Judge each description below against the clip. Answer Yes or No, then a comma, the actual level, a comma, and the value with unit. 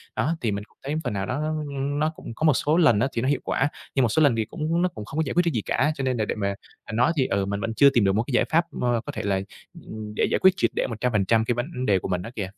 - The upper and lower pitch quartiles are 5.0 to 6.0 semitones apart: Yes, average, 5.3 semitones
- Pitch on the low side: Yes, low, 120 Hz